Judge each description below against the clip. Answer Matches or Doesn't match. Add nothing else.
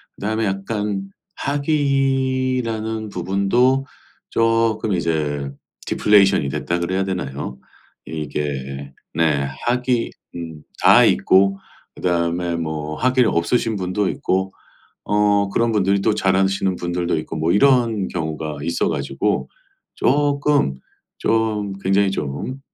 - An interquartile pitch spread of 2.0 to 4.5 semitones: Doesn't match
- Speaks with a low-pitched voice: Matches